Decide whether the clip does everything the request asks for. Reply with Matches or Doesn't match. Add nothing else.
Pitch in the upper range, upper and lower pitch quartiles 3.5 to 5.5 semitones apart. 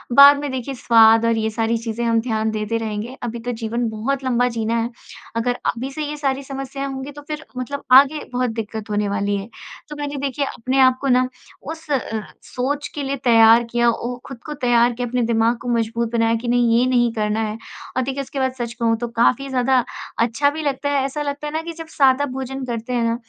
Doesn't match